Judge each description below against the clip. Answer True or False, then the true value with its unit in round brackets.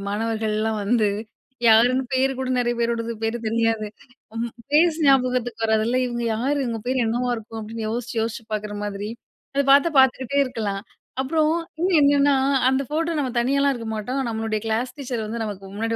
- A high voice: True (235 Hz)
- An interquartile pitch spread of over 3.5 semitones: False (3.0 semitones)